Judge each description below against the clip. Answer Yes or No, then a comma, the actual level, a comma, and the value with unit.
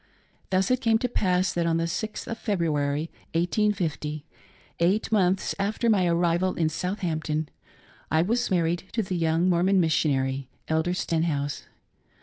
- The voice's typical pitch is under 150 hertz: No, medium, 175 Hz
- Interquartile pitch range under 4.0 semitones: Yes, average, 3.3 semitones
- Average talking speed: Yes, average, 150 wpm